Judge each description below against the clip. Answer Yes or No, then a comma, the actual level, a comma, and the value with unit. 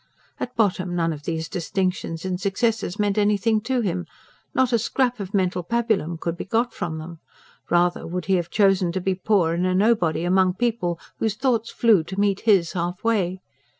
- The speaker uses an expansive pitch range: No, average, 3.9 semitones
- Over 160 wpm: Yes, average, 190 wpm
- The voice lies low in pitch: No, high, 190 Hz